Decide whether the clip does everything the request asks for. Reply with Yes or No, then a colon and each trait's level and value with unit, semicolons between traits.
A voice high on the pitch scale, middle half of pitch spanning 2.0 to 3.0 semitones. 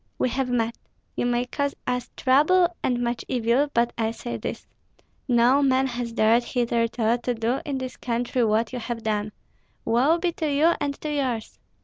Yes: high, 245 Hz; average, 2.7 semitones